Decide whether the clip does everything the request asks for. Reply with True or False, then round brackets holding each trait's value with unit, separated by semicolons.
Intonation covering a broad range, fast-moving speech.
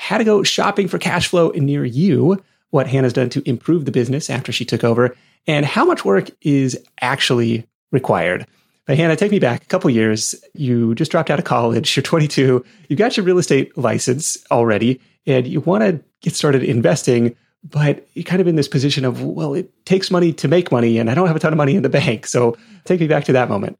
True (5.7 semitones; 225 wpm)